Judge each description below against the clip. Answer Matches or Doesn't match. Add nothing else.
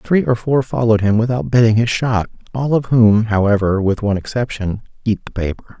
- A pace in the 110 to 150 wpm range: Doesn't match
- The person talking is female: Doesn't match